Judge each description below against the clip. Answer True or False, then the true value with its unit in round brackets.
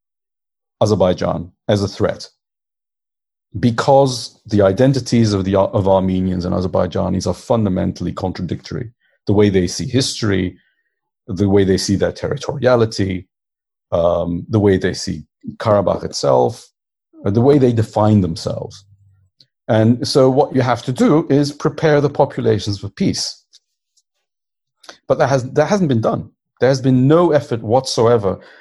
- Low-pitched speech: True (110 Hz)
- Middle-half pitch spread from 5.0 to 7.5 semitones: True (5.5 semitones)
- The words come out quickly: False (135 wpm)